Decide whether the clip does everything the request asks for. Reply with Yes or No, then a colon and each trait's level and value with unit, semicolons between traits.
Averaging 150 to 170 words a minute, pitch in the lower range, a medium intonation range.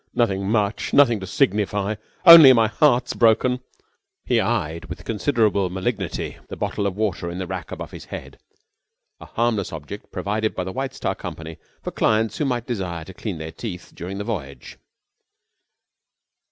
Yes: average, 165 wpm; low, 105 Hz; average, 4.2 semitones